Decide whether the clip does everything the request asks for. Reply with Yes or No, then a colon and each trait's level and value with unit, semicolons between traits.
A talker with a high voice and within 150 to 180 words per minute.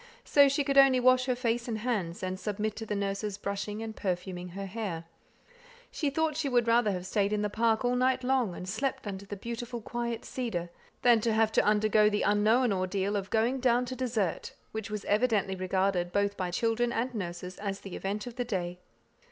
No: high, 215 Hz; fast, 205 wpm